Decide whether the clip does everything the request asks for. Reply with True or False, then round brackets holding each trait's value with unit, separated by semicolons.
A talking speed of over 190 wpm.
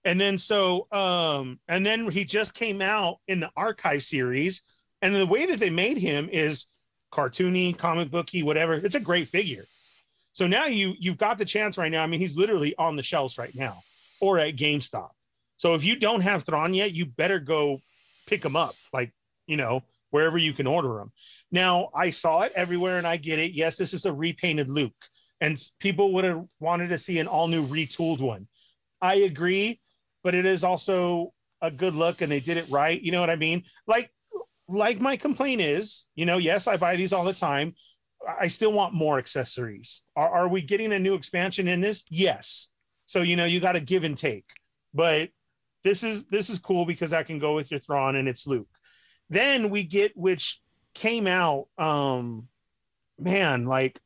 True (200 wpm)